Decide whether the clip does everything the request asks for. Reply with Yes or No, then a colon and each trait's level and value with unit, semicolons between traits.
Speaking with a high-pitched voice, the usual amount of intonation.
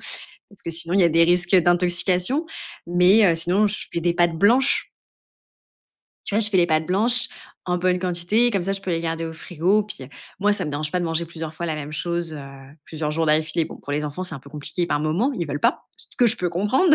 No: medium, 175 Hz; average, 3.4 semitones